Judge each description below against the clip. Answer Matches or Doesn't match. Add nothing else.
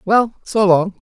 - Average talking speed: Matches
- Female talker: Doesn't match